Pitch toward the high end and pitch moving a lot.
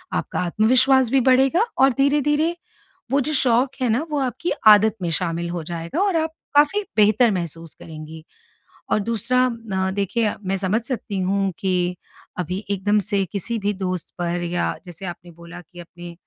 Yes: high, 200 Hz; wide, 6.3 semitones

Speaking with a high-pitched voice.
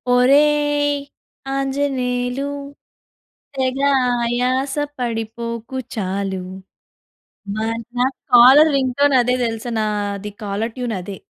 Yes: high, 245 Hz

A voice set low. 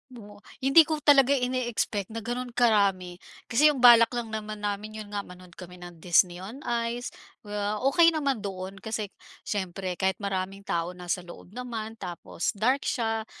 No: high, 215 Hz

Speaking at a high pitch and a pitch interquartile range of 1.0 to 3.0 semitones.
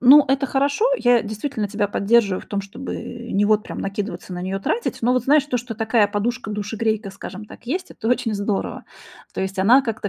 No: high, 220 Hz; average, 3.6 semitones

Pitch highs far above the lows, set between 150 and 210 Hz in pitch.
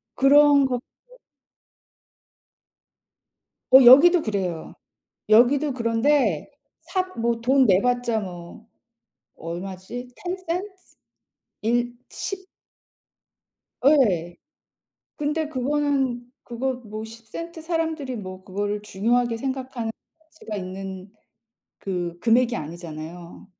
No: wide, 5.7 semitones; high, 240 Hz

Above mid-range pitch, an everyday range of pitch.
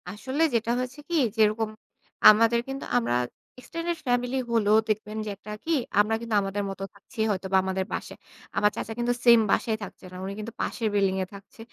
Yes: high, 220 Hz; average, 3.2 semitones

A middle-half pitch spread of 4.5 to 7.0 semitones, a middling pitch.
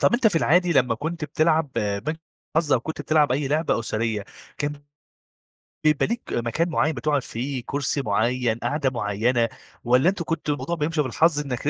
Yes: average, 4.8 semitones; medium, 145 Hz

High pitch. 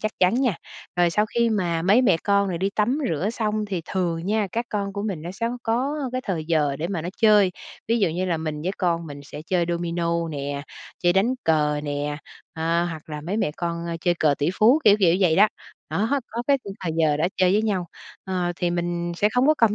No: medium, 180 Hz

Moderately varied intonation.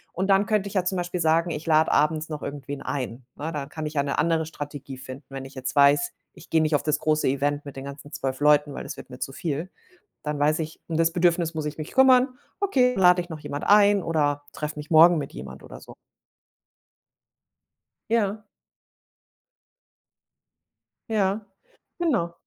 Yes: average, 3.6 semitones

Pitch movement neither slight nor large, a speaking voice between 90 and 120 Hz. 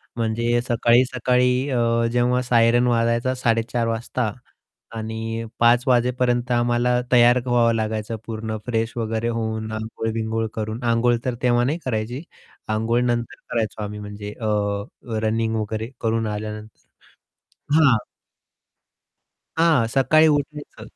No: narrow, 1.7 semitones; low, 115 Hz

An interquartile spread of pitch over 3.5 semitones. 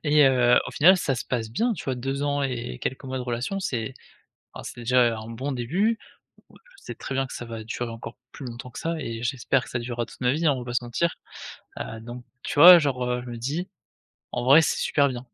No: average, 3.0 semitones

